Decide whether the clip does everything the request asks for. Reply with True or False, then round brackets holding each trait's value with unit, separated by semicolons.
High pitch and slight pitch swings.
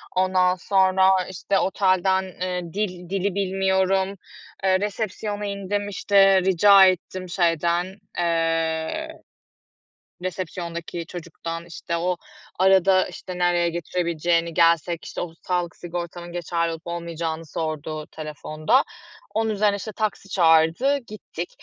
False (180 Hz; 2.3 semitones)